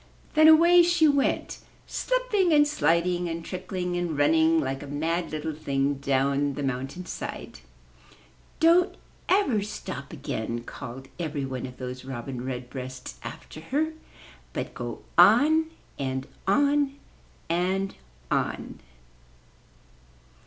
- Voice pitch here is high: No, medium, 165 Hz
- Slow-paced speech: Yes, slow, 125 wpm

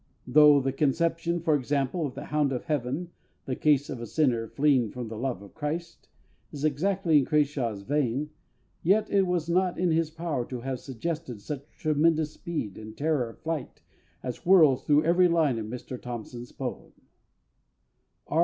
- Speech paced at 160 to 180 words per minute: Yes, average, 170 wpm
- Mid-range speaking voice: Yes, medium, 145 Hz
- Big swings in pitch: No, average, 4.5 semitones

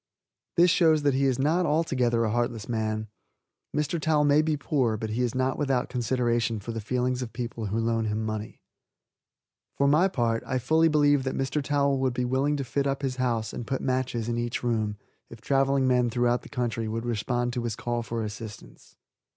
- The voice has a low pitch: Yes, low, 125 Hz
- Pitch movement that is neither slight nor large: Yes, average, 3.3 semitones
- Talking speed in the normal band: No, fast, 210 wpm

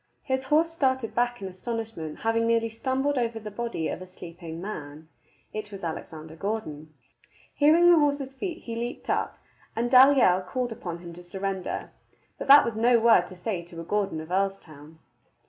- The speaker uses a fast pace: No, average, 180 wpm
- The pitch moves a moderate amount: No, wide, 6.0 semitones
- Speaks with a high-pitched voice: Yes, high, 215 Hz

